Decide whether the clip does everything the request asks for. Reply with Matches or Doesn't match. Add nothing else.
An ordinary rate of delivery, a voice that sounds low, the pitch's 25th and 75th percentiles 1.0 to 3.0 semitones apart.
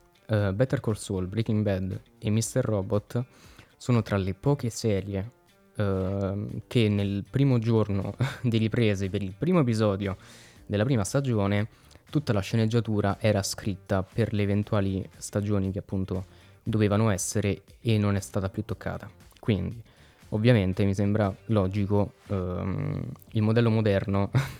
Matches